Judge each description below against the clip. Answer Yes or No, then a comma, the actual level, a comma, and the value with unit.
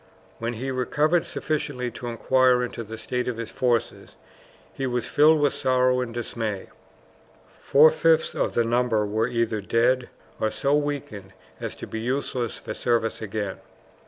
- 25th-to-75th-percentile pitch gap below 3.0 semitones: Yes, narrow, 2.6 semitones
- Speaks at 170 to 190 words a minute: No, average, 160 wpm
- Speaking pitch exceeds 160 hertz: No, low, 125 Hz